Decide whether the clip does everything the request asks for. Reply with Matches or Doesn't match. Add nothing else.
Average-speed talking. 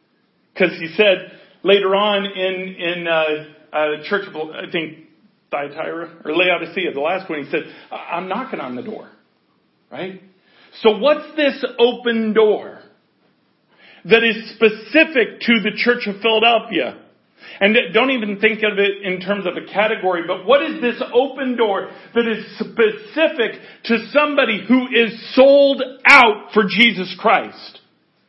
Matches